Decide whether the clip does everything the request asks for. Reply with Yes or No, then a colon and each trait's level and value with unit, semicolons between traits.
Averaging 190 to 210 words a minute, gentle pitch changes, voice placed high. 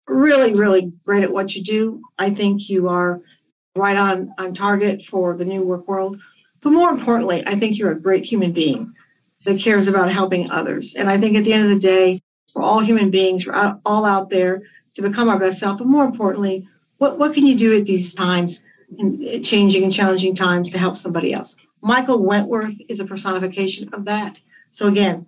Yes: fast, 205 wpm; narrow, 2.2 semitones; high, 195 Hz